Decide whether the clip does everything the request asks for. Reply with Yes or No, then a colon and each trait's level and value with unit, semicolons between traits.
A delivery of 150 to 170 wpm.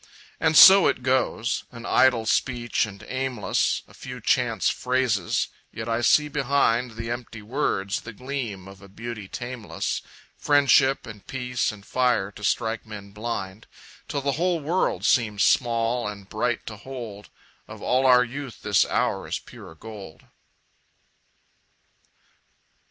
No: average, 140 wpm